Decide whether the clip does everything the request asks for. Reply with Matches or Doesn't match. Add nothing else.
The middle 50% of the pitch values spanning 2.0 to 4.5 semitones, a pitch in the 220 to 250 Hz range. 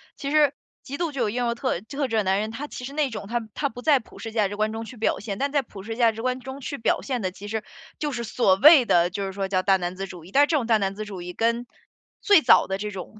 Doesn't match